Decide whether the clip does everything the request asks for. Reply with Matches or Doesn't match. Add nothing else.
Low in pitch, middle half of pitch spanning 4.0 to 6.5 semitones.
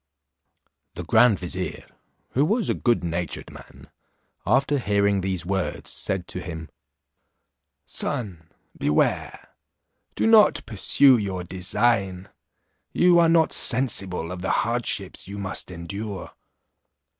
Matches